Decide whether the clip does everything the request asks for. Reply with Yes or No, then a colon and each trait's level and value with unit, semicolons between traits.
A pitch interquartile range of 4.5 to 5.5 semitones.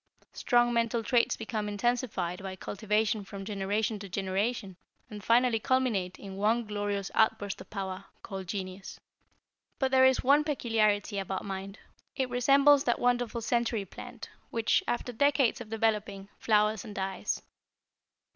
No: average, 3.5 semitones